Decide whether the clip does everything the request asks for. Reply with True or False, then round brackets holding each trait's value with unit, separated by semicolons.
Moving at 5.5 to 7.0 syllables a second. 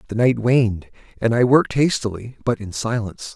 True (5.7 syllables/s)